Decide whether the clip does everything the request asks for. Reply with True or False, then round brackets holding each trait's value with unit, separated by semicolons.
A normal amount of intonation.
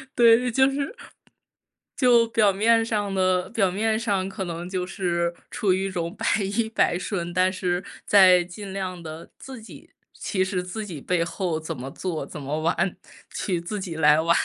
True (3.5 semitones)